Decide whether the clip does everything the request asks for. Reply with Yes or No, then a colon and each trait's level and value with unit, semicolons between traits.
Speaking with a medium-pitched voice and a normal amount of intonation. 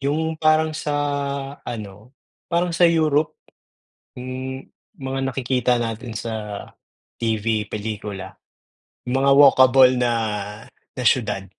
No: low, 130 Hz; average, 4.3 semitones